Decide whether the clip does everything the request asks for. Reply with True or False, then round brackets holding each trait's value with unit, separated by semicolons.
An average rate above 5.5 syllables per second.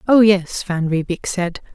False (4.0 syllables/s)